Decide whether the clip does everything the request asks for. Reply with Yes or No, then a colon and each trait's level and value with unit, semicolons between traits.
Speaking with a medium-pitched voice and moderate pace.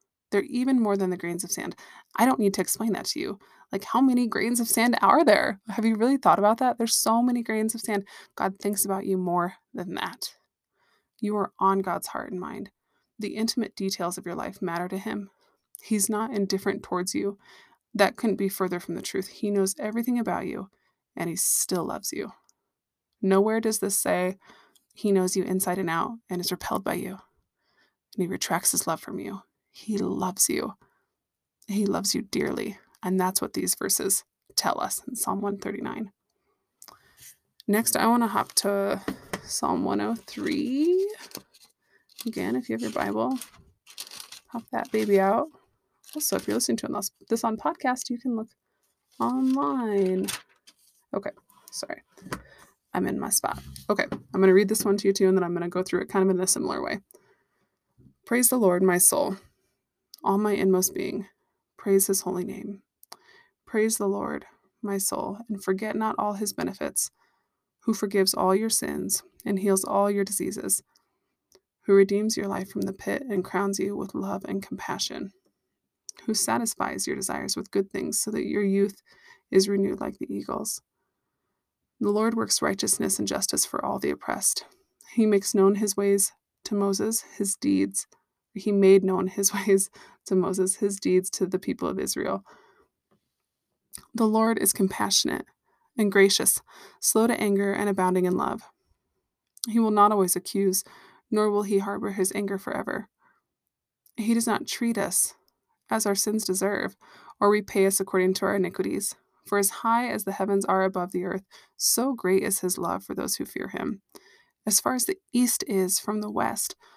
No: high, 200 Hz; average, 180 wpm